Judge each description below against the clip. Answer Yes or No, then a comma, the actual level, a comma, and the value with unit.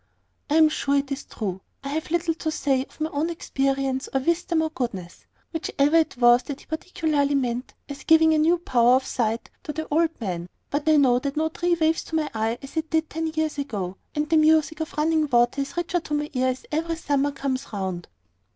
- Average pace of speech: No, fast, 225 wpm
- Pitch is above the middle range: Yes, very high, 290 Hz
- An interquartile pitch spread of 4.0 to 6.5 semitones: No, average, 3.6 semitones